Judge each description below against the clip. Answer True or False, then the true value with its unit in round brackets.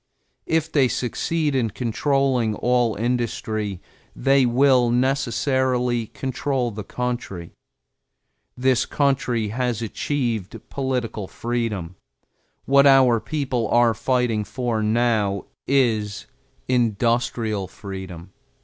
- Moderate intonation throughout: True (3.2 semitones)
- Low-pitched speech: True (120 Hz)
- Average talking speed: False (95 wpm)